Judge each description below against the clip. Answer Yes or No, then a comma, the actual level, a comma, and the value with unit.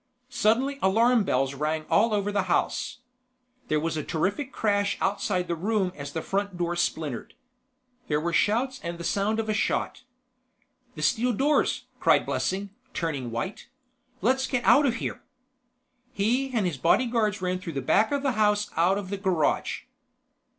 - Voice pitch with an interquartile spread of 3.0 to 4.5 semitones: No, average, 5.2 semitones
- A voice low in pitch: No, high, 200 Hz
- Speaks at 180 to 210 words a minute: No, average, 165 wpm